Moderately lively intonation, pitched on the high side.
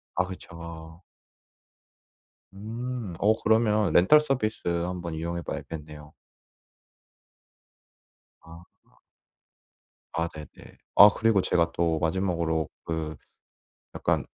No: average, 4.3 semitones; very low, 85 Hz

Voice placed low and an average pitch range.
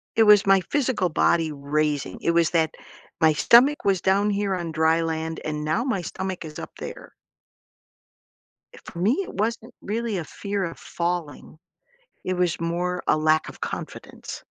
No: medium, 175 Hz; average, 4.0 semitones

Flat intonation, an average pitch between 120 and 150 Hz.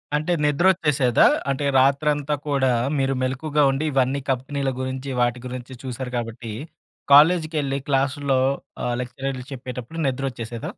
Yes: narrow, 2.2 semitones; low, 135 Hz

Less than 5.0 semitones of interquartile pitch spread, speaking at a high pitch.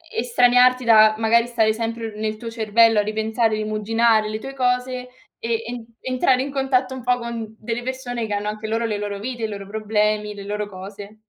Yes: narrow, 2.4 semitones; high, 225 Hz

